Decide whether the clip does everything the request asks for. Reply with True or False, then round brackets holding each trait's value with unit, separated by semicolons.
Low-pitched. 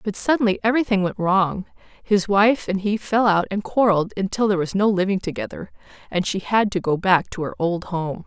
False (195 Hz)